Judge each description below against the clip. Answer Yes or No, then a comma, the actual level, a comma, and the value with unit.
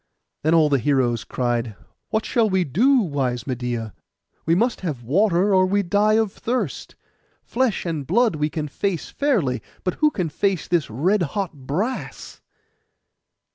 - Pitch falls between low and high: Yes, medium, 170 Hz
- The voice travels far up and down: Yes, wide, 7.1 semitones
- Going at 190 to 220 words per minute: No, average, 155 wpm